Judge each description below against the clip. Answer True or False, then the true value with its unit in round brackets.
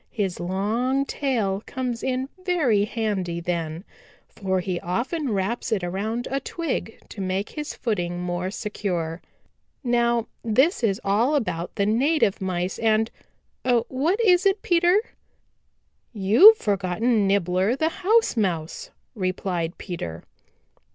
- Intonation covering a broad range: True (5.8 semitones)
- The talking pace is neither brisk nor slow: False (125 wpm)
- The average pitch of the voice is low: False (215 Hz)